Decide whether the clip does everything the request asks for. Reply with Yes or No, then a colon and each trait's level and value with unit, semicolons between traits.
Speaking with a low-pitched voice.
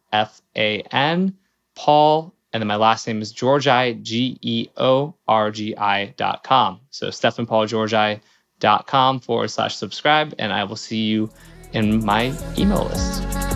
Yes: low, 110 Hz